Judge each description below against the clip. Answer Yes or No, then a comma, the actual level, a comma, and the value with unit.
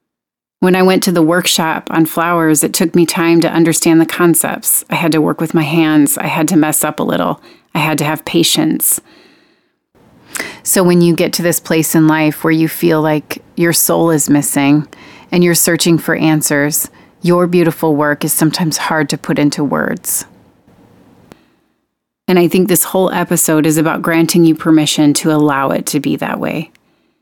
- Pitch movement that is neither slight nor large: No, narrow, 1.9 semitones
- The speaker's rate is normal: Yes, average, 185 wpm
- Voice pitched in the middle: Yes, medium, 165 Hz